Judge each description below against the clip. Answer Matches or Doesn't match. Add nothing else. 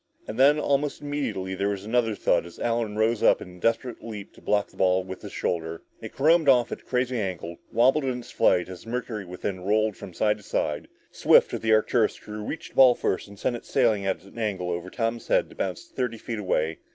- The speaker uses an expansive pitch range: Doesn't match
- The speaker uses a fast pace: Matches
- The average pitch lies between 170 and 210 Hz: Doesn't match